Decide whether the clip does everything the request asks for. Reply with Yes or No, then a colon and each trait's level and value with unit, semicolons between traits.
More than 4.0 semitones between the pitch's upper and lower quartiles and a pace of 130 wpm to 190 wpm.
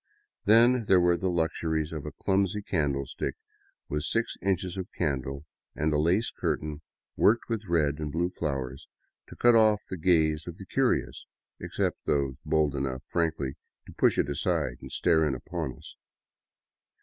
Yes: average, 4.7 semitones; average, 160 wpm